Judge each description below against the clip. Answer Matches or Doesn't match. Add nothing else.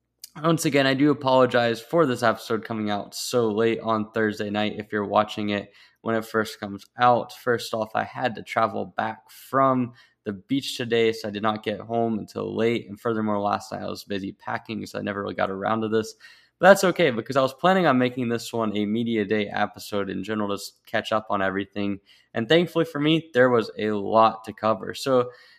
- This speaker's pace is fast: Matches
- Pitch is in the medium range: Doesn't match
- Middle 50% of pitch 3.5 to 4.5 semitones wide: Doesn't match